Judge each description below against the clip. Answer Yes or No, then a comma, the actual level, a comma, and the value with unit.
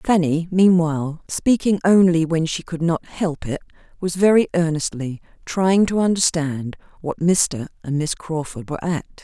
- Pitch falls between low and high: Yes, medium, 165 Hz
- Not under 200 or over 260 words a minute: No, average, 150 wpm